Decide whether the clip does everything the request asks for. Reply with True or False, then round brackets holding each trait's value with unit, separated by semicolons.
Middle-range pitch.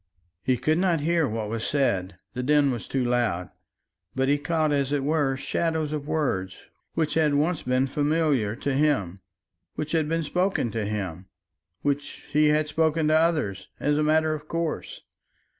True (145 Hz)